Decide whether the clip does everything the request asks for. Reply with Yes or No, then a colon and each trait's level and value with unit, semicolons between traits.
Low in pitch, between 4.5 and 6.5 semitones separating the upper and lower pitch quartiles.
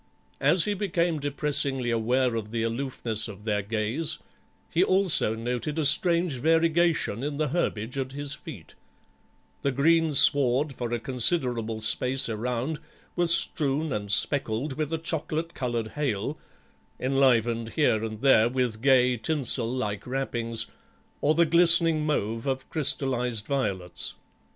Yes: low, 130 Hz; average, 5.0 semitones